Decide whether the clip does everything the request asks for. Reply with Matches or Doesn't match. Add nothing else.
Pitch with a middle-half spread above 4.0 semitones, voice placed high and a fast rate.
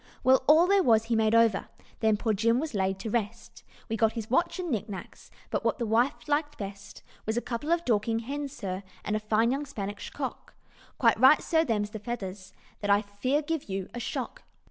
Matches